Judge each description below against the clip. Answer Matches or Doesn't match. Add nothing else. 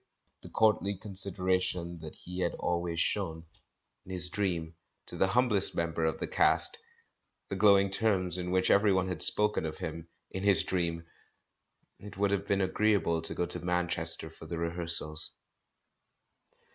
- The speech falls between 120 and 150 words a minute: Doesn't match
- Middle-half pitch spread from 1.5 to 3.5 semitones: Matches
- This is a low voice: Matches